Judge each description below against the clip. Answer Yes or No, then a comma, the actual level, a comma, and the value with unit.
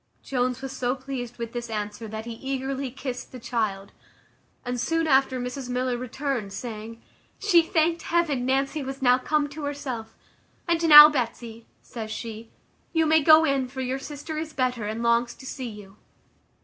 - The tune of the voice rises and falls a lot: No, average, 3.4 semitones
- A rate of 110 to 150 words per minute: No, average, 175 wpm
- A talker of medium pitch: No, very high, 255 Hz